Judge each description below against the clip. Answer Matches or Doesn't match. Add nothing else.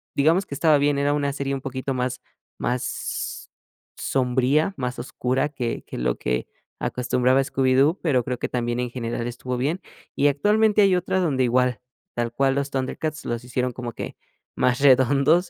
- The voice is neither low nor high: Doesn't match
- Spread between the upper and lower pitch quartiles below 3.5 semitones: Matches